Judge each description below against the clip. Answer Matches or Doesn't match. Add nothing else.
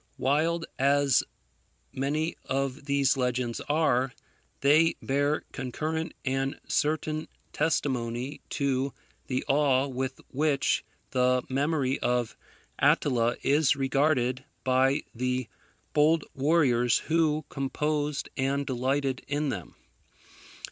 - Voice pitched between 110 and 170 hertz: Matches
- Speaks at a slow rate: Matches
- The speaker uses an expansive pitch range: Doesn't match